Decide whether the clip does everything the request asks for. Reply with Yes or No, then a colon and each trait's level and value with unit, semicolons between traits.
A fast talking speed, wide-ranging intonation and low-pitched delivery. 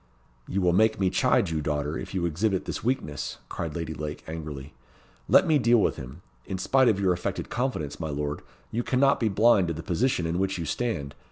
Yes: fast, 210 wpm; wide, 6.3 semitones; very low, 90 Hz